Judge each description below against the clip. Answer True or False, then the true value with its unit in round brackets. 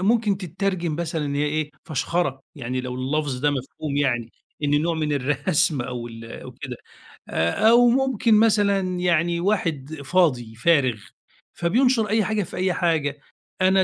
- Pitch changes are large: True (5.8 semitones)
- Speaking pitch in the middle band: True (155 Hz)